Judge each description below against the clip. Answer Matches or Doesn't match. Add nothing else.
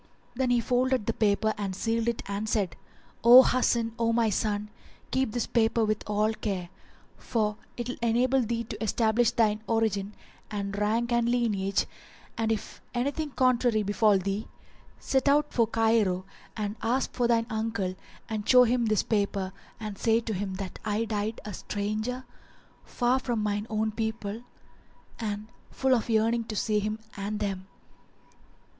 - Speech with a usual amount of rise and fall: Doesn't match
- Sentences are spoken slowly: Doesn't match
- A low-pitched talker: Doesn't match